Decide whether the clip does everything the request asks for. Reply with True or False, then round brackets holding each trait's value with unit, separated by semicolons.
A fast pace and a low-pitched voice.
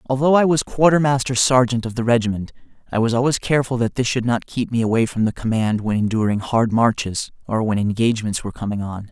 True (210 wpm; 115 Hz)